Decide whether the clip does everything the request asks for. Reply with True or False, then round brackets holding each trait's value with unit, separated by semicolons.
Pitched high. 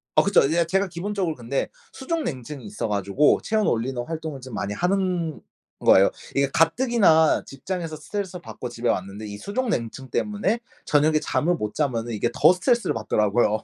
False (155 Hz)